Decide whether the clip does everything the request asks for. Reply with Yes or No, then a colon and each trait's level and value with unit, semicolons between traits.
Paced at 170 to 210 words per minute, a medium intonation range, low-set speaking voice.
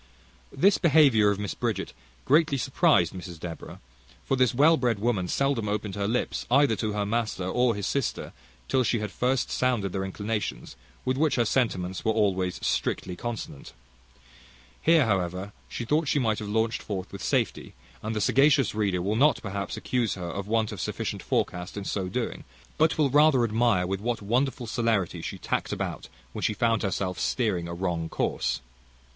Yes: average, 175 wpm; average, 4.7 semitones; low, 110 Hz